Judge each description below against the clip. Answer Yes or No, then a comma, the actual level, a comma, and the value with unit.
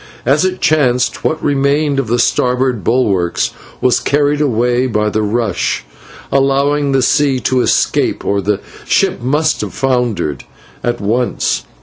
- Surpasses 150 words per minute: No, average, 140 wpm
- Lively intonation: No, average, 3.4 semitones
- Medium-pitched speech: No, low, 125 Hz